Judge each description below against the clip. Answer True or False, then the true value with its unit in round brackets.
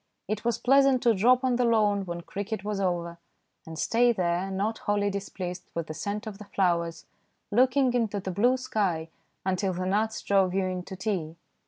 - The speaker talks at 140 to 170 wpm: False (190 wpm)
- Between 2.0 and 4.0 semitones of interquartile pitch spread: True (3.7 semitones)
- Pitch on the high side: True (200 Hz)